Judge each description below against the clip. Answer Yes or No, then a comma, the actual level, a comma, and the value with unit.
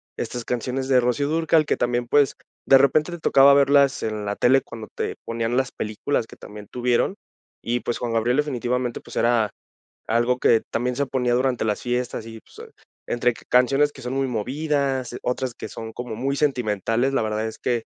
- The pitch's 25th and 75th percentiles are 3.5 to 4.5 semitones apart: No, average, 2.8 semitones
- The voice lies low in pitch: Yes, low, 125 Hz